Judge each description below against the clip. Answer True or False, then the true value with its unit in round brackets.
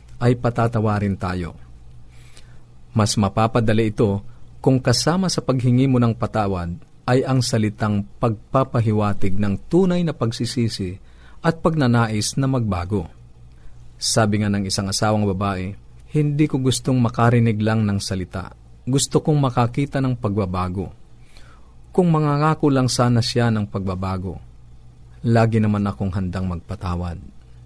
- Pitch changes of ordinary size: True (4.6 semitones)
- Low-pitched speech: True (110 Hz)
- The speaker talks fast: False (120 wpm)